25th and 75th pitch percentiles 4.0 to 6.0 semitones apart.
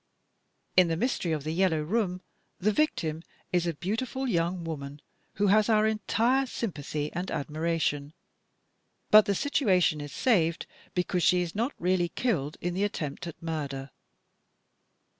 Yes: average, 5.1 semitones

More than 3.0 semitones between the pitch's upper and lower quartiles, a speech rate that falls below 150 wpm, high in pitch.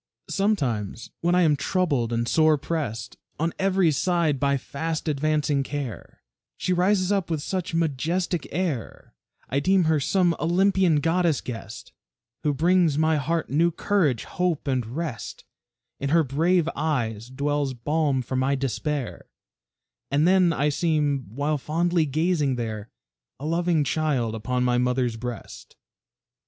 No: average, 4.4 semitones; average, 140 wpm; medium, 150 Hz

